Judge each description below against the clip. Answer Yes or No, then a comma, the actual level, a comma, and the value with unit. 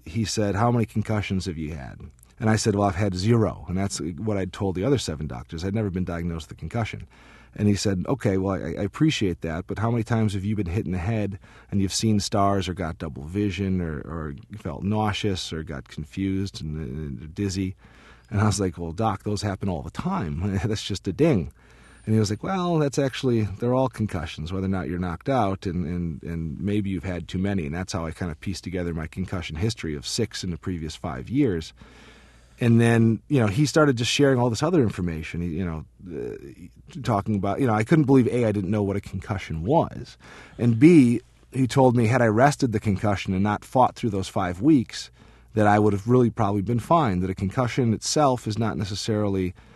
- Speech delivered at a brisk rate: Yes, fast, 225 wpm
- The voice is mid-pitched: No, low, 100 Hz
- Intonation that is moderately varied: Yes, average, 3.8 semitones